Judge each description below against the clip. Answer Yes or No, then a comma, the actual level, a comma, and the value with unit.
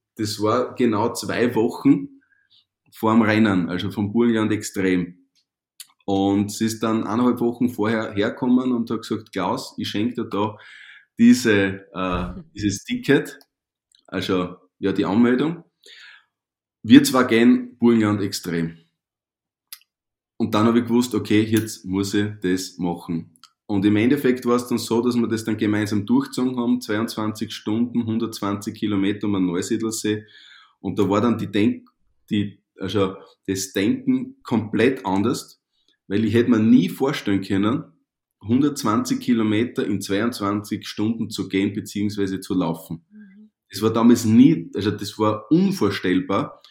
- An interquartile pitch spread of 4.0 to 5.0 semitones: No, average, 3.3 semitones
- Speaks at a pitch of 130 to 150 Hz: No, low, 110 Hz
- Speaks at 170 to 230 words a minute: No, average, 140 wpm